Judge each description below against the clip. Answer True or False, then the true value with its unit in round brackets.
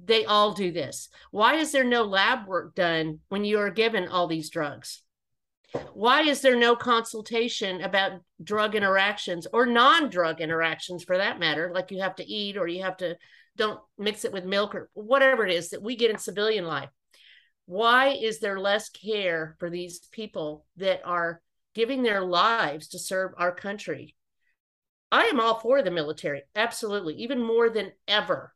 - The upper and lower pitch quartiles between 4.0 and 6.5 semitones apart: True (4.3 semitones)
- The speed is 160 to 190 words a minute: True (180 wpm)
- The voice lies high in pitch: True (200 Hz)